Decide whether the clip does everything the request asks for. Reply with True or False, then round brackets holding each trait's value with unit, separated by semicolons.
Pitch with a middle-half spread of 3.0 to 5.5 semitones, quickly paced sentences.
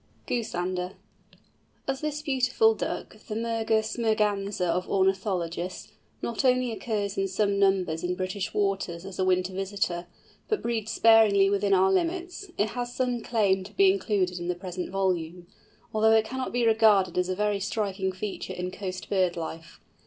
False (3.3 semitones; 160 wpm)